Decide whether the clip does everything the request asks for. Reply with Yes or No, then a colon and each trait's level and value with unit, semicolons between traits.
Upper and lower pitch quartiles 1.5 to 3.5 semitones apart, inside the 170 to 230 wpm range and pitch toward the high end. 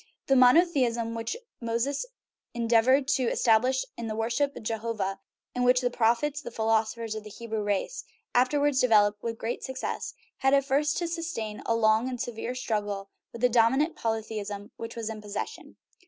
Yes: average, 3.0 semitones; average, 175 wpm; high, 230 Hz